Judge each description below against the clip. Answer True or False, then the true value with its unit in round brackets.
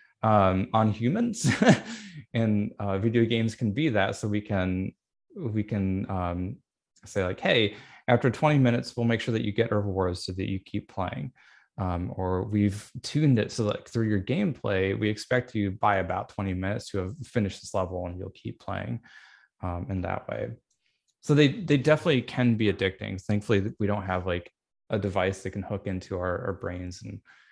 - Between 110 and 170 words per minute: False (190 wpm)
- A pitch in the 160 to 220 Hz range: False (105 Hz)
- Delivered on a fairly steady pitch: False (3.7 semitones)